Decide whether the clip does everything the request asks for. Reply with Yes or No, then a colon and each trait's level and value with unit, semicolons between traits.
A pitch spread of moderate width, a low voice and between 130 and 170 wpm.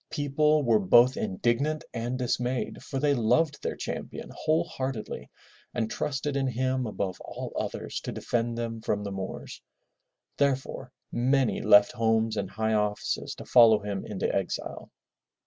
Yes: average, 3.7 semitones; low, 120 Hz; average, 145 wpm